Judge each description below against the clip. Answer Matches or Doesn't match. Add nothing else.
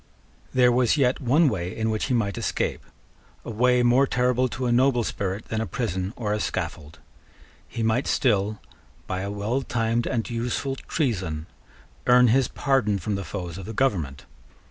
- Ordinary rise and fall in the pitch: Matches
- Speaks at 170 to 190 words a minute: Matches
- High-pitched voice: Doesn't match